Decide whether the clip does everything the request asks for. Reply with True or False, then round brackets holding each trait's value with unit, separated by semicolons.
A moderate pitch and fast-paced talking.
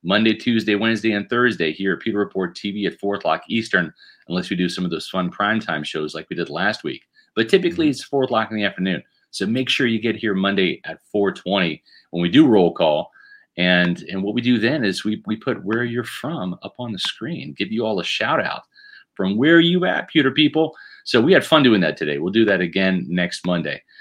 False (105 Hz; 230 wpm)